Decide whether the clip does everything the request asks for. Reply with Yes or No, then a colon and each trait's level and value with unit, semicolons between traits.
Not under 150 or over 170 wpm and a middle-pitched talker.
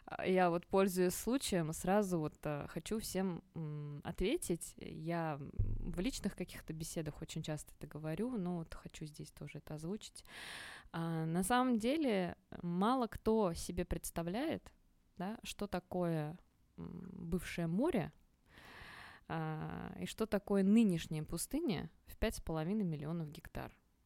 No: average, 120 wpm; medium, 180 Hz